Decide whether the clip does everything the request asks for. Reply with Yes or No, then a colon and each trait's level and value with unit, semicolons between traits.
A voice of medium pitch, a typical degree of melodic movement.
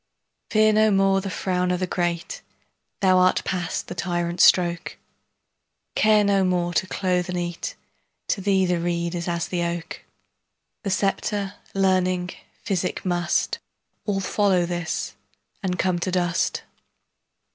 No: medium, 180 Hz; narrow, 1.8 semitones